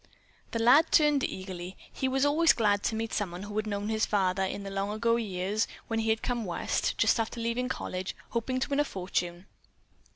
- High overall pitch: Yes, high, 220 Hz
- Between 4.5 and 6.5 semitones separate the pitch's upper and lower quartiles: No, average, 3.5 semitones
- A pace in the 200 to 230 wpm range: Yes, fast, 205 wpm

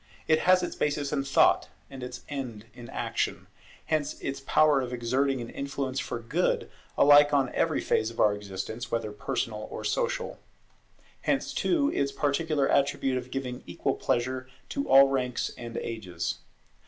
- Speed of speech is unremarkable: Yes, average, 160 wpm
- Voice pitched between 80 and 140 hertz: Yes, low, 135 Hz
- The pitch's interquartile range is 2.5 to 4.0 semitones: Yes, average, 3.4 semitones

